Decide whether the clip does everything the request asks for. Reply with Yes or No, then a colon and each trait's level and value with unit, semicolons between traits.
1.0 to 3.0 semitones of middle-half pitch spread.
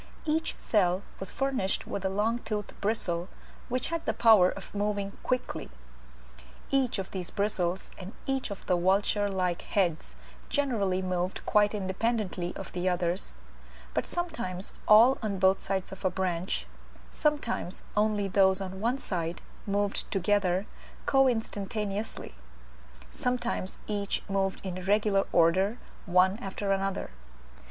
Yes: average, 2.7 semitones